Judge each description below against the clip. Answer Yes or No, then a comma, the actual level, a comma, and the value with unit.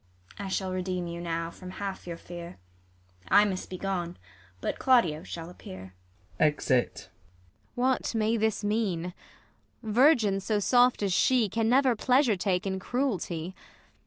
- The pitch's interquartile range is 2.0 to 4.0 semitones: No, average, 4.5 semitones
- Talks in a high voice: Yes, high, 195 Hz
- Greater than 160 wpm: No, average, 145 wpm